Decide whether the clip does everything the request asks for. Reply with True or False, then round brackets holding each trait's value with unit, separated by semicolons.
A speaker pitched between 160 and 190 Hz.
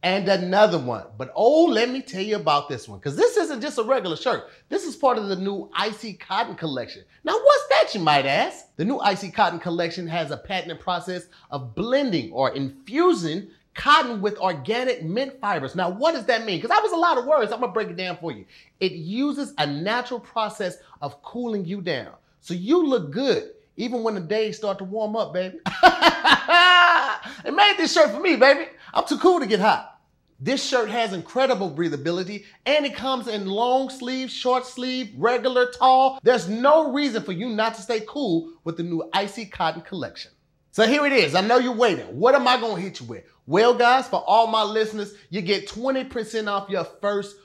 False (220 Hz)